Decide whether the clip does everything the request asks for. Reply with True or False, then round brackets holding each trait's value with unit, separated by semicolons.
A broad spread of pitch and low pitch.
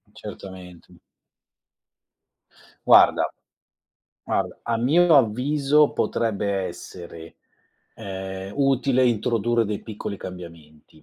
True (5.7 semitones; 105 Hz)